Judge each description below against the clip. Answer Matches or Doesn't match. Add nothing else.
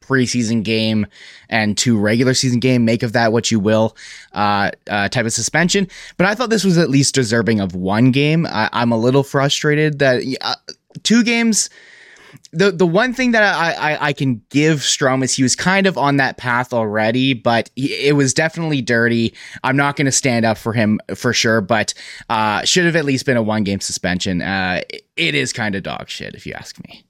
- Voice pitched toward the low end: Matches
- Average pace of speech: Doesn't match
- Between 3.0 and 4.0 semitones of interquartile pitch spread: Doesn't match